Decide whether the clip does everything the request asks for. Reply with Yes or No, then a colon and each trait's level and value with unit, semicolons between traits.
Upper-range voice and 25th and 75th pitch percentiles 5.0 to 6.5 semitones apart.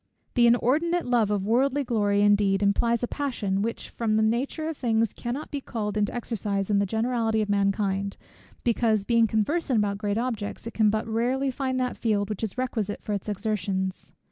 No: high, 220 Hz; average, 3.1 semitones